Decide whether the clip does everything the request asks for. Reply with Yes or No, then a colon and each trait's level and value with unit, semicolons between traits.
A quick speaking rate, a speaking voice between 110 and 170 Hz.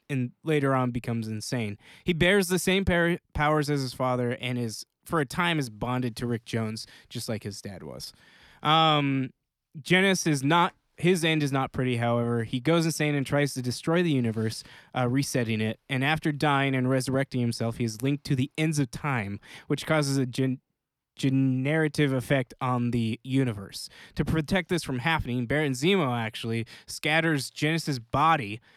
No: average, 175 wpm; low, 135 Hz